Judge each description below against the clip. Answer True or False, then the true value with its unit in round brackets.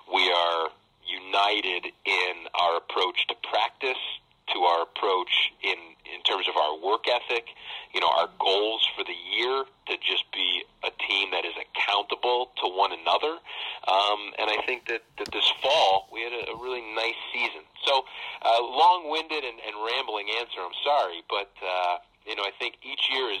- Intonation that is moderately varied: True (4.7 semitones)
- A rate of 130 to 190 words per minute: True (175 wpm)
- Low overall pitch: True (110 Hz)